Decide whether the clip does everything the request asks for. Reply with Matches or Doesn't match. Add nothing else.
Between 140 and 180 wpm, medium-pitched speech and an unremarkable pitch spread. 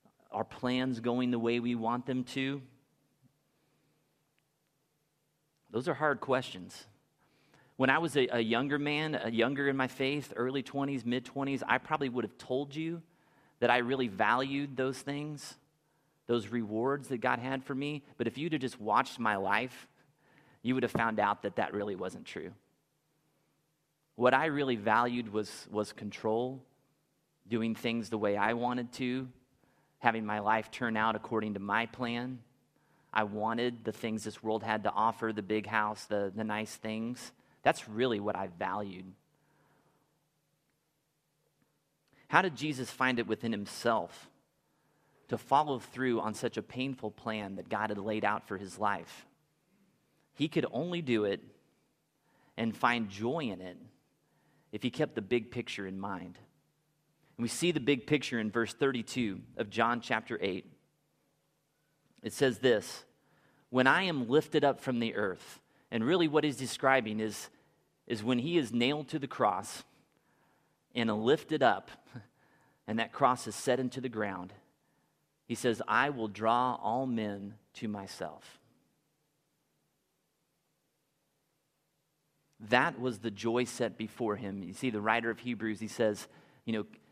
Doesn't match